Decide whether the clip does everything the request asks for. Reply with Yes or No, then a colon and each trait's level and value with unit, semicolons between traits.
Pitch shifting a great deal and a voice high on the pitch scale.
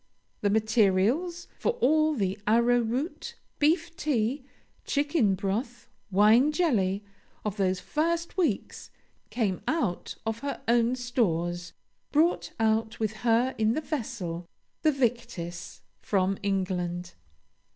Yes: wide, 6.7 semitones; high, 230 Hz